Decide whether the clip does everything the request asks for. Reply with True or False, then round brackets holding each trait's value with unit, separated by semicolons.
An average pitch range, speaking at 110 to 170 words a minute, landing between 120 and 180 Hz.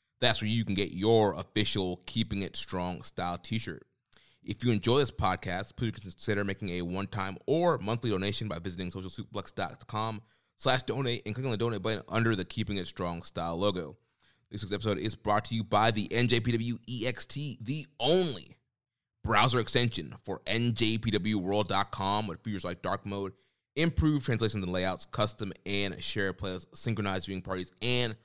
False (3.3 semitones; 160 wpm; 105 Hz)